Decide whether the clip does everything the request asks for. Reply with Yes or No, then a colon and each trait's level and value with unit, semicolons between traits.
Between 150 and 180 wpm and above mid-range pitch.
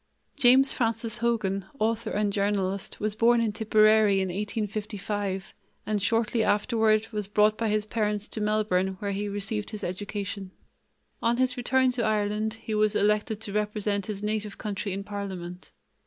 Yes: average, 155 wpm; high, 210 Hz